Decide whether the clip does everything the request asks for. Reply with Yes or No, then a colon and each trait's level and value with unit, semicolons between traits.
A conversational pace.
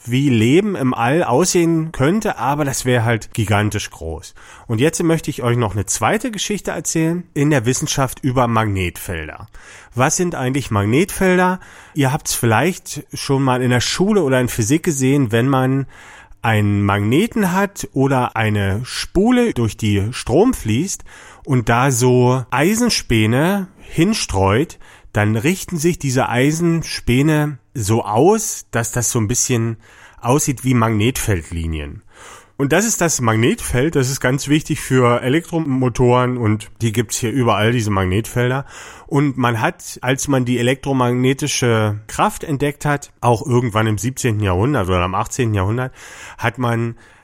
Yes: average, 150 wpm